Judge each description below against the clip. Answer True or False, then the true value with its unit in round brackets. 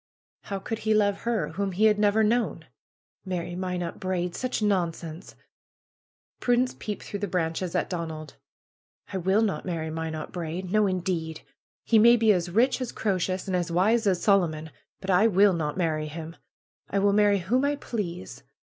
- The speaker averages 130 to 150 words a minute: False (170 wpm)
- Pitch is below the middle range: False (190 Hz)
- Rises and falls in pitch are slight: False (3.8 semitones)